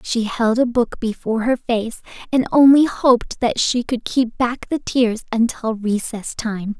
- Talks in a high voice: Yes, high, 235 Hz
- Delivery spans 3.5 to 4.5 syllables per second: Yes, 4.2 syllables/s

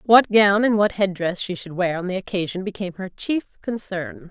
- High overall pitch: Yes, high, 195 Hz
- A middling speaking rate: No, fast, 225 wpm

